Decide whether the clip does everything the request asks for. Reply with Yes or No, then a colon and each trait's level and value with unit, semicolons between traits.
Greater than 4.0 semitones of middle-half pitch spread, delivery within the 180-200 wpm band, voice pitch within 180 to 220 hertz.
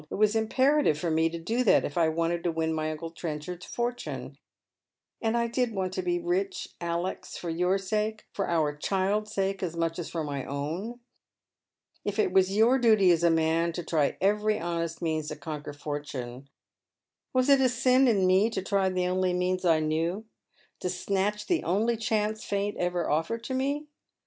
Yes: average, 4.7 semitones; average, 195 wpm; medium, 185 Hz